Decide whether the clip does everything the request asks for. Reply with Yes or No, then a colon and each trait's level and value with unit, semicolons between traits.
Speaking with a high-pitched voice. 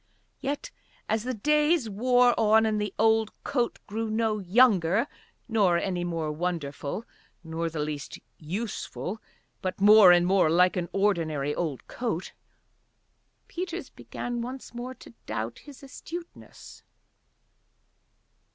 Yes: high, 210 Hz